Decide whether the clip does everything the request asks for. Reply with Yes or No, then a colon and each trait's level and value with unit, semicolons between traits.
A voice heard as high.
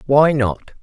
No: low, 135 Hz